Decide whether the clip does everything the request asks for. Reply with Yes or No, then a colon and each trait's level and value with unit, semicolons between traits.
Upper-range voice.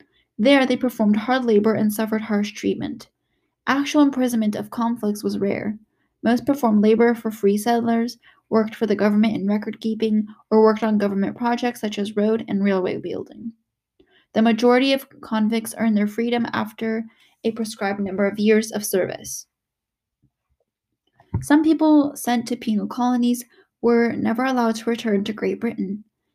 Yes: high, 225 Hz